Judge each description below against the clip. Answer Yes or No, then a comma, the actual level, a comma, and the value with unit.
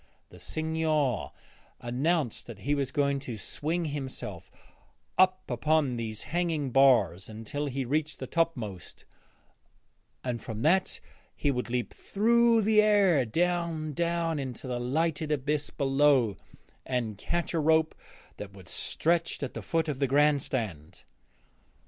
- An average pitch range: Yes, average, 4.9 semitones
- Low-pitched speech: No, medium, 145 Hz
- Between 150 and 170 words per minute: No, slow, 135 wpm